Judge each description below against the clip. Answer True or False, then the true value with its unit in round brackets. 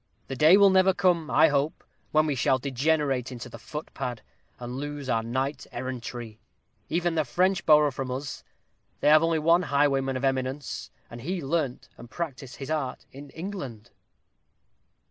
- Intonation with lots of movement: False (3.7 semitones)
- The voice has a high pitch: False (140 Hz)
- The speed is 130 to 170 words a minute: True (165 wpm)